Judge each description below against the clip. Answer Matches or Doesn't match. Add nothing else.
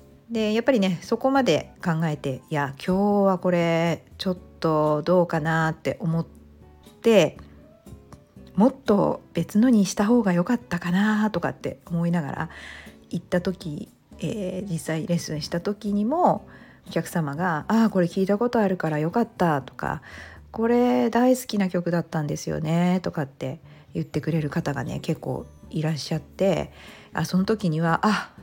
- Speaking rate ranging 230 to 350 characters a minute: Matches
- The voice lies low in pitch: Doesn't match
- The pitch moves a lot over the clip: Doesn't match